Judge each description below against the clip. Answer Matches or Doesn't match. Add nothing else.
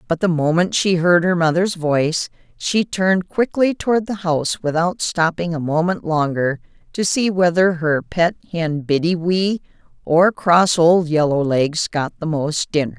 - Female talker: Matches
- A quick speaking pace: Doesn't match